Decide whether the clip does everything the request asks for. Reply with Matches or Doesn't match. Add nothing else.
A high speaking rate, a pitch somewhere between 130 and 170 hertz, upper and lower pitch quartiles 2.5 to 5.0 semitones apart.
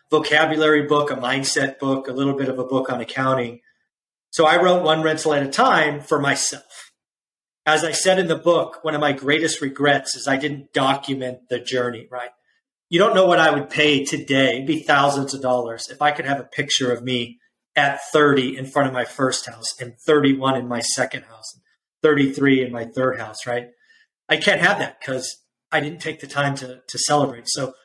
Matches